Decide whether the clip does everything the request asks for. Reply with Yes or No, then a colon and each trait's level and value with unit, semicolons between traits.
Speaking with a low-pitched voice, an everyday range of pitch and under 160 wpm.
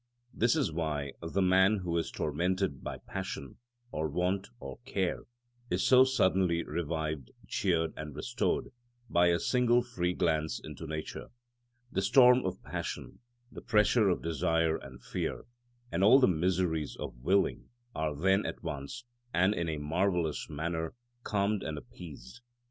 Yes: very low, 85 Hz; average, 3.9 semitones; average, 150 wpm